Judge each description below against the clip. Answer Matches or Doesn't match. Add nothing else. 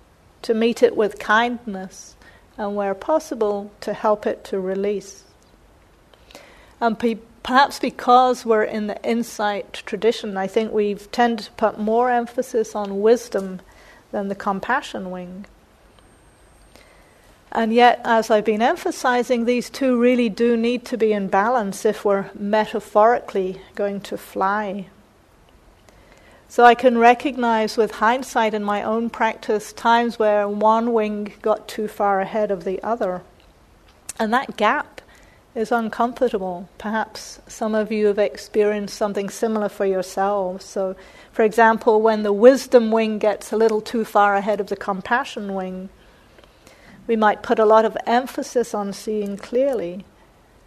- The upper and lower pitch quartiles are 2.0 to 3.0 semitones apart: Matches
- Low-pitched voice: Doesn't match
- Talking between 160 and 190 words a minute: Doesn't match